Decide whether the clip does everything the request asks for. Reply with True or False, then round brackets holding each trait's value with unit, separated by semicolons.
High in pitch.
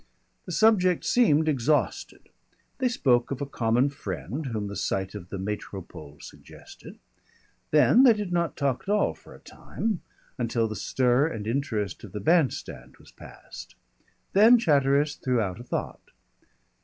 False (135 Hz)